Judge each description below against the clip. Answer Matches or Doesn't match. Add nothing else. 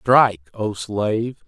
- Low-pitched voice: Matches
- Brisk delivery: Doesn't match